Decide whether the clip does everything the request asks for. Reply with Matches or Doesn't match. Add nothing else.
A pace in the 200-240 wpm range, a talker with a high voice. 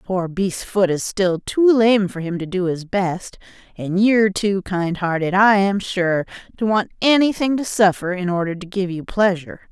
Matches